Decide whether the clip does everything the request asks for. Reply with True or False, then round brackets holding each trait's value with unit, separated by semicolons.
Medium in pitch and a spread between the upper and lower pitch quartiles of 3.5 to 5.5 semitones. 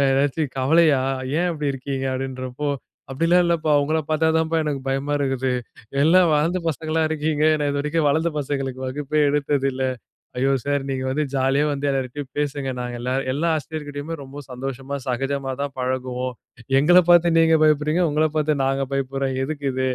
False (145 Hz; 2.6 semitones)